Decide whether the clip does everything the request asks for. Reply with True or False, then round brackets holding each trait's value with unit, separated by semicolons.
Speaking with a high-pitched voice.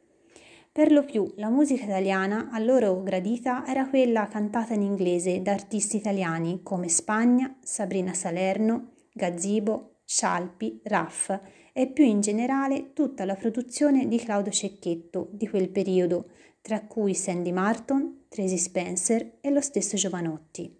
True (210 Hz)